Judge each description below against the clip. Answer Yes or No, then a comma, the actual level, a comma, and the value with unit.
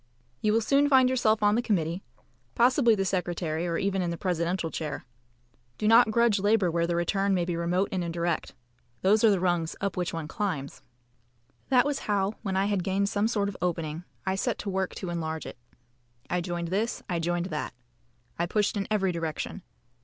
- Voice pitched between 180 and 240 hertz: Yes, high, 190 Hz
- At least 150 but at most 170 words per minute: No, average, 200 wpm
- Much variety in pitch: No, average, 3.5 semitones